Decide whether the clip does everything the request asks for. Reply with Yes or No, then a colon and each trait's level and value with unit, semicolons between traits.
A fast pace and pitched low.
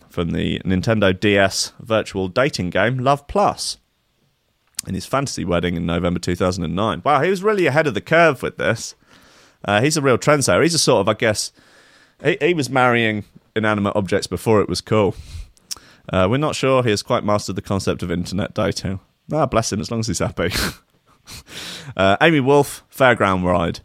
No: average, 185 wpm; low, 105 Hz